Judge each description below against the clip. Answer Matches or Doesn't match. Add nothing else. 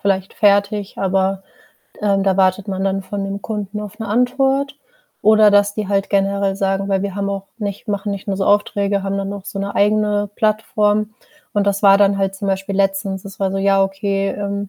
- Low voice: Doesn't match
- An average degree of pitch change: Doesn't match